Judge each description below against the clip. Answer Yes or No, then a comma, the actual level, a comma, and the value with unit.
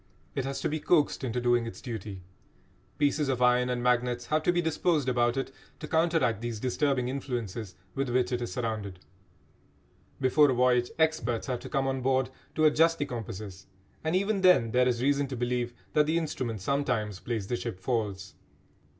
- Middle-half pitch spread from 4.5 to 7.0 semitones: No, average, 3.4 semitones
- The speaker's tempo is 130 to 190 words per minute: Yes, average, 185 wpm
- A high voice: No, low, 125 Hz